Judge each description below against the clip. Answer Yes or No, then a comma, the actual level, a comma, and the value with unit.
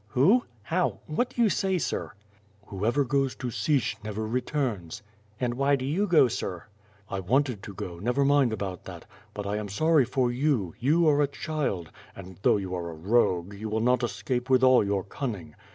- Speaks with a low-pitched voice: Yes, low, 120 Hz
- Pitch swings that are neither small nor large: No, wide, 5.9 semitones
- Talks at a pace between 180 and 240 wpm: Yes, average, 195 wpm